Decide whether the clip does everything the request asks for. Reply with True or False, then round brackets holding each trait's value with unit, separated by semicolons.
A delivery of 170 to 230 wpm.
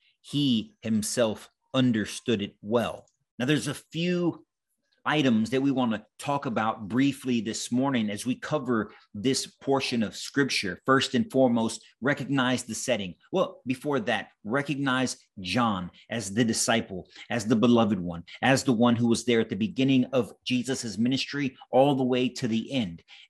False (160 wpm)